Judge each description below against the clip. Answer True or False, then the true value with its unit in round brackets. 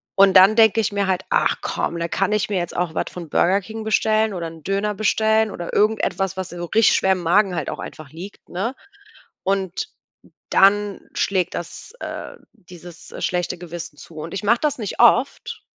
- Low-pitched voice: False (195 Hz)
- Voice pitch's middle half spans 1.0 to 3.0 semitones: False (3.6 semitones)